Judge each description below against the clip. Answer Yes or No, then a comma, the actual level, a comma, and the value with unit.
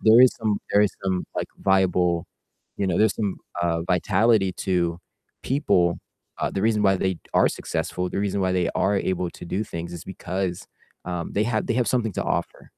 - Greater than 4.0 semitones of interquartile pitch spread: No, average, 3.0 semitones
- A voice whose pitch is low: Yes, very low, 95 Hz